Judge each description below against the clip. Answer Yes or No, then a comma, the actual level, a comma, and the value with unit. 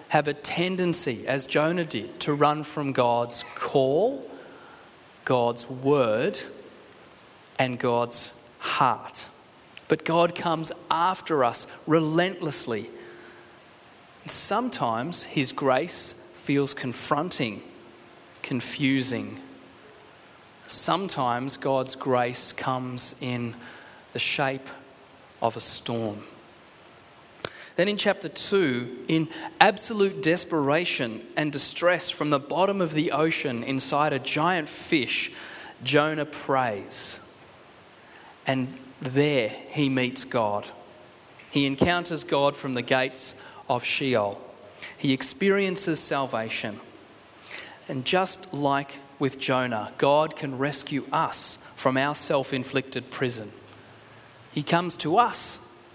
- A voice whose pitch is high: No, low, 135 Hz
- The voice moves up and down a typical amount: Yes, average, 3.8 semitones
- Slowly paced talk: Yes, slow, 100 wpm